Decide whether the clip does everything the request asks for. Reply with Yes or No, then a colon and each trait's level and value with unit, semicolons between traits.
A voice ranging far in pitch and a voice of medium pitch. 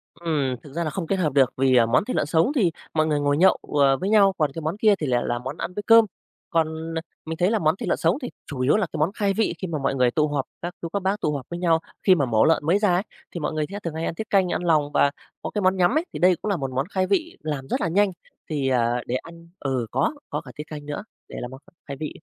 No: average, 4.8 semitones; medium, 160 Hz